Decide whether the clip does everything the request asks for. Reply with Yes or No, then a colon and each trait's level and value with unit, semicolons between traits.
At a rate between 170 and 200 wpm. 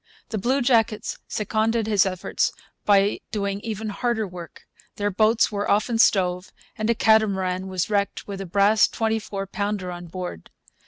No: average, 155 wpm